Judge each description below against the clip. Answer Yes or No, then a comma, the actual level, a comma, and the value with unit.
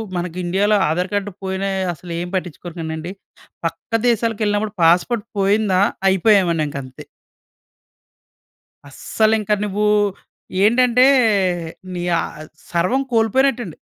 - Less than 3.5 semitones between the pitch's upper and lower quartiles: No, average, 4.0 semitones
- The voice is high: Yes, high, 195 Hz